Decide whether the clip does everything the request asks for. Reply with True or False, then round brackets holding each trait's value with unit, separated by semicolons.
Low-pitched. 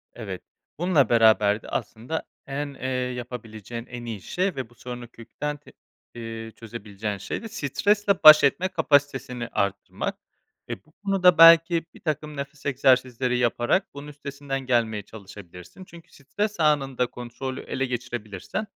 True (130 Hz)